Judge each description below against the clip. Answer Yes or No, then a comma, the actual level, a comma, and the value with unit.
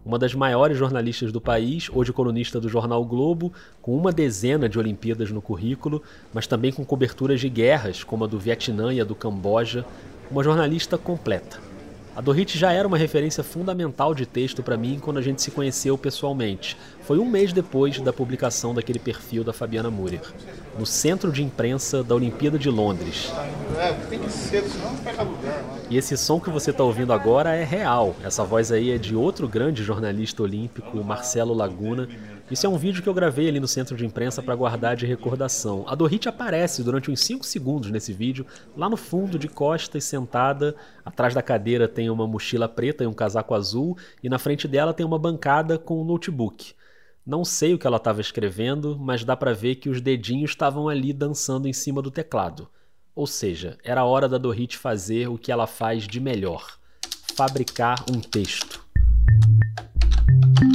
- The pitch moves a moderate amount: Yes, average, 4.2 semitones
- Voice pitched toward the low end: Yes, low, 125 Hz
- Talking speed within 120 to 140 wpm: No, average, 180 wpm